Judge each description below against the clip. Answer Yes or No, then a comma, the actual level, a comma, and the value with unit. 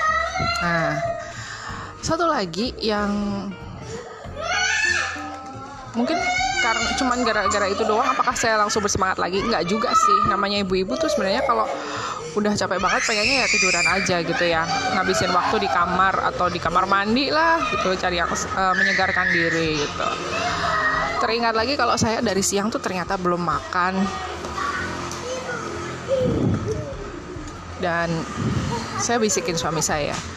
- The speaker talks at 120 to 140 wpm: Yes, average, 125 wpm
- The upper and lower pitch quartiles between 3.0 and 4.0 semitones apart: No, average, 5.3 semitones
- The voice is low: No, high, 205 Hz